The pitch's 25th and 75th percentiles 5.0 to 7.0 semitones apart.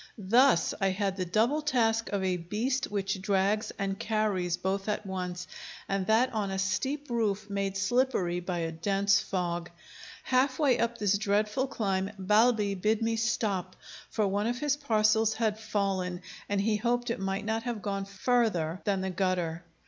No: average, 3.0 semitones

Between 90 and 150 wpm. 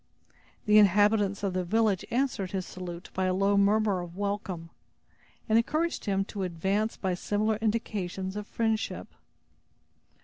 Yes: average, 140 wpm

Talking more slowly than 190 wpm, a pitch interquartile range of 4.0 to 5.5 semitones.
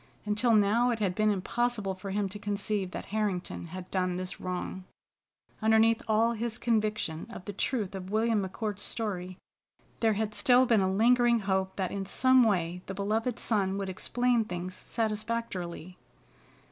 No: average, 160 wpm; average, 3.2 semitones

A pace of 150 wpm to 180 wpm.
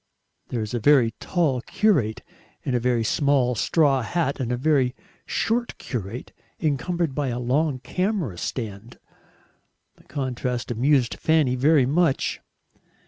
No: slow, 135 wpm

